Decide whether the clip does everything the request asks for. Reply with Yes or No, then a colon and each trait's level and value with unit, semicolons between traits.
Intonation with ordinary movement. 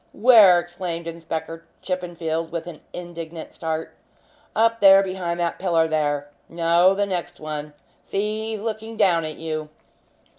Yes: average, 3.1 semitones